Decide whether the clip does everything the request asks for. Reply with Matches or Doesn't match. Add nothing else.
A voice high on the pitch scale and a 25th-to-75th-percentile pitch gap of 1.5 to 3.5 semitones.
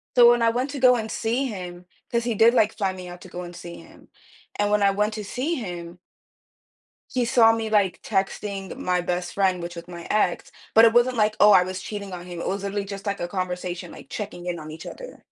Doesn't match